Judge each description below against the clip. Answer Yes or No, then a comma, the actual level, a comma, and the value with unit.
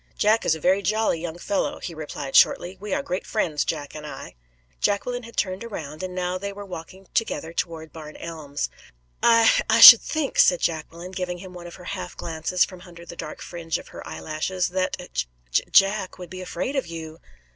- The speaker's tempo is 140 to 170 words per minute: No, average, 200 wpm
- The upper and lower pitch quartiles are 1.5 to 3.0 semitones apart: No, average, 3.4 semitones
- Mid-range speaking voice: Yes, medium, 180 Hz